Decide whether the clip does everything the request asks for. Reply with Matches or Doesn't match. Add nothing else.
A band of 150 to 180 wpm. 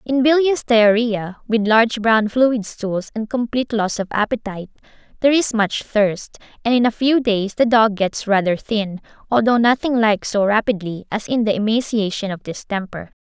Matches